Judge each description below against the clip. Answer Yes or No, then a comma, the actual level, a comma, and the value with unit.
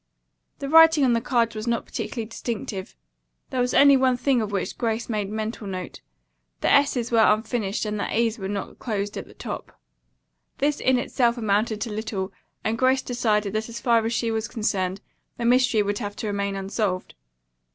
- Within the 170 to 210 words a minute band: Yes, average, 190 wpm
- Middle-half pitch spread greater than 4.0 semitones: No, average, 3.0 semitones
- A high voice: Yes, high, 225 Hz